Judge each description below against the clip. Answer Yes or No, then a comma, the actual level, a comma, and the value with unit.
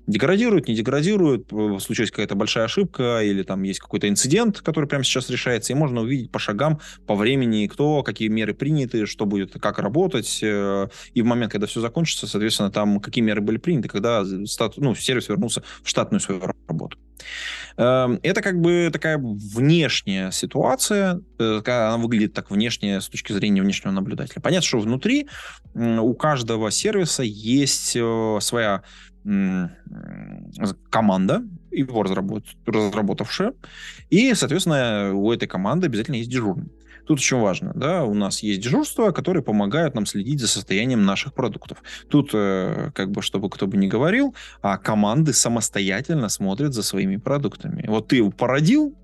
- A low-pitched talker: Yes, low, 120 Hz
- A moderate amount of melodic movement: No, wide, 7.6 semitones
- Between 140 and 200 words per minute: Yes, average, 150 wpm